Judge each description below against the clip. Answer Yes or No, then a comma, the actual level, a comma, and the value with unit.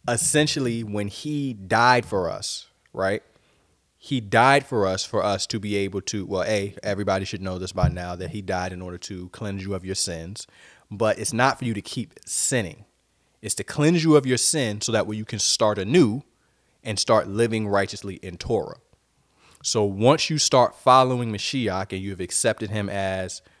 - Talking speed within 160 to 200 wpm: Yes, average, 190 wpm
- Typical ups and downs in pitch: Yes, average, 4.3 semitones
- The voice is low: Yes, low, 105 Hz